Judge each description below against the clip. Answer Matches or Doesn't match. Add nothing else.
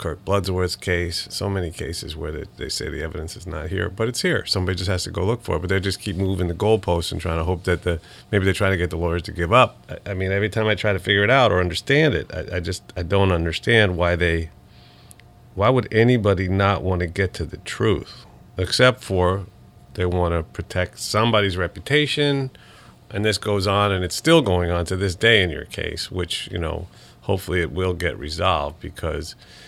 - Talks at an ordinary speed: Doesn't match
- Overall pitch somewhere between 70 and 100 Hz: Matches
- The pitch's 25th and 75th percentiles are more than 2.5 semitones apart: Matches